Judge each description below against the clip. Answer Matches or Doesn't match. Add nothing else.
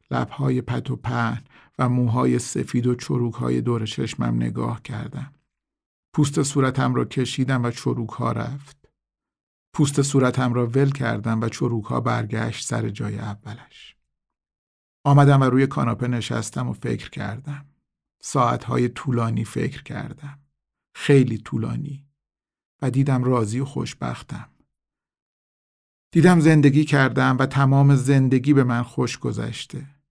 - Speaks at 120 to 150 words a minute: Matches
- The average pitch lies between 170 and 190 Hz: Doesn't match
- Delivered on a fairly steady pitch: Doesn't match